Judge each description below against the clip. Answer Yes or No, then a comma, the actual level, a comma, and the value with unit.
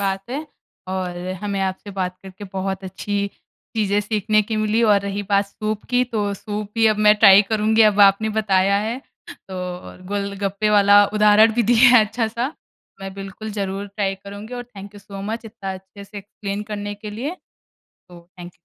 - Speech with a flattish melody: Yes, narrow, 1.7 semitones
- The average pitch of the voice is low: No, high, 205 Hz